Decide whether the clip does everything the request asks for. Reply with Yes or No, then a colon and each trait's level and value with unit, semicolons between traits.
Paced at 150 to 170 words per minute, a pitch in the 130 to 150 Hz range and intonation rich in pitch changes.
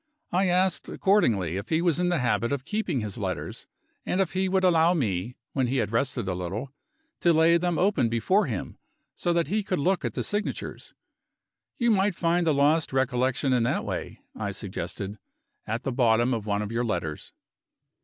No: average, 195 wpm; medium, 140 Hz; wide, 7.6 semitones